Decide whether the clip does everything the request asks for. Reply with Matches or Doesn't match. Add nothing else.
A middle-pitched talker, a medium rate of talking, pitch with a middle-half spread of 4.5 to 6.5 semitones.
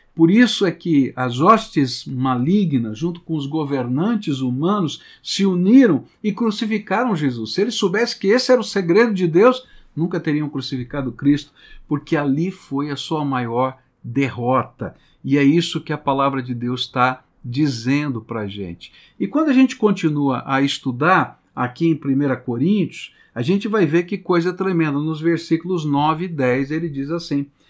Matches